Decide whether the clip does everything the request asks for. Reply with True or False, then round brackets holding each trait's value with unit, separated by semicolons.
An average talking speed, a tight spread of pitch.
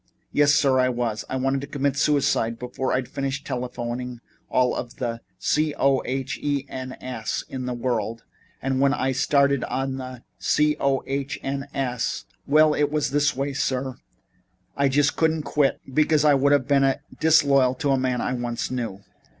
True (175 wpm; 2.0 semitones)